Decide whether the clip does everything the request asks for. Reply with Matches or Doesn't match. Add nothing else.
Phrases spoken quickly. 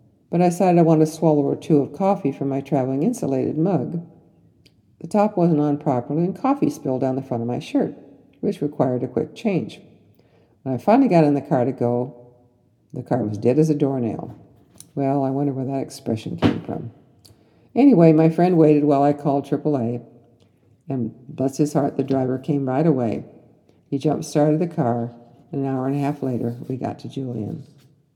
Doesn't match